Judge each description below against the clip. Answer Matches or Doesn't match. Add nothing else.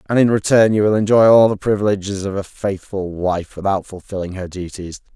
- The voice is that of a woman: Doesn't match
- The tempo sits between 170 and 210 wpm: Matches